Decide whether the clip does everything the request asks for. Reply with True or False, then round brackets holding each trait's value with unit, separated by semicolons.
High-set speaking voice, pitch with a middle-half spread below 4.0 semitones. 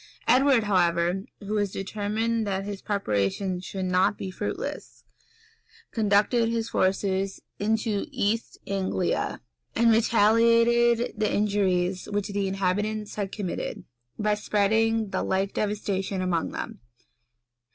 True (205 Hz; 2.6 semitones)